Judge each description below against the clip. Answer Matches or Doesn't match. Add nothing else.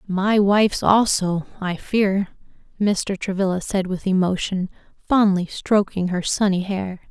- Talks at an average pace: Doesn't match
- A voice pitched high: Matches